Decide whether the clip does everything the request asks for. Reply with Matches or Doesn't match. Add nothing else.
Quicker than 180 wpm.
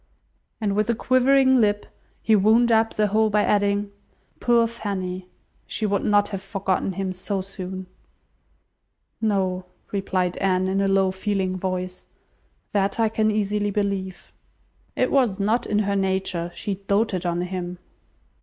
Doesn't match